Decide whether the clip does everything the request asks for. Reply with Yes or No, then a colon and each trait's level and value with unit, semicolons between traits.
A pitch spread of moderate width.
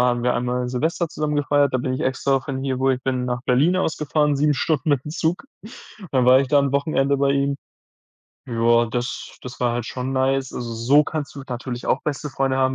No: narrow, 2.3 semitones